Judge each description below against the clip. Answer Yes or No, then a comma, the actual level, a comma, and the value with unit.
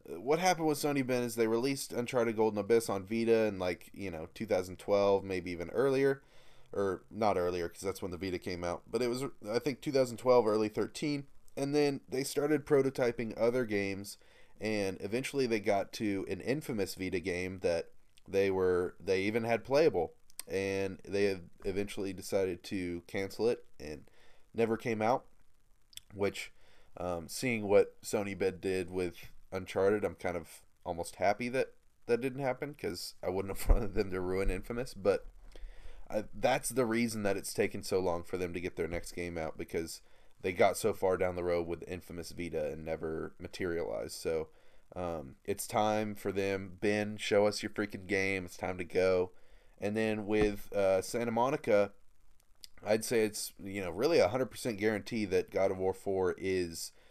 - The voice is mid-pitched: No, low, 105 Hz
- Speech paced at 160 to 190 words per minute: Yes, average, 180 wpm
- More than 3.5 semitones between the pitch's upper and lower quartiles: Yes, average, 4.1 semitones